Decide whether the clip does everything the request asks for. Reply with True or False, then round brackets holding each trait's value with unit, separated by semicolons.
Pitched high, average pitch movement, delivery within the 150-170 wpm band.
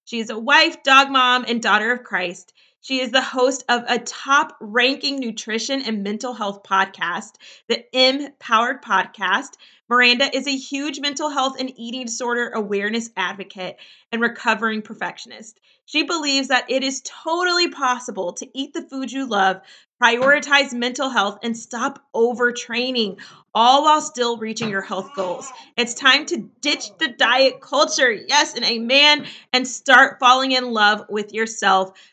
True (245 Hz; 3.6 semitones; 155 wpm)